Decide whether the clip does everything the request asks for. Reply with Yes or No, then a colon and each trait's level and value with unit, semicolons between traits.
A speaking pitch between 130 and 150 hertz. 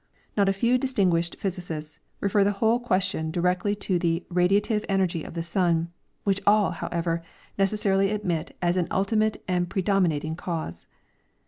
No: medium, 185 Hz